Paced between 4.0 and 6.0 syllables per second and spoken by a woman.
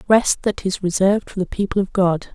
Yes: 5.6 syllables/s; female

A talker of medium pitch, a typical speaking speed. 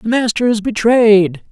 No: high, 220 Hz; average, 160 wpm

